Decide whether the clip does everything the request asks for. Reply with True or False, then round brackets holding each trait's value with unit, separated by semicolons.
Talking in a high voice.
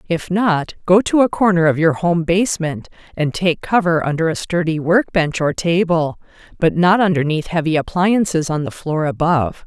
False (170 Hz)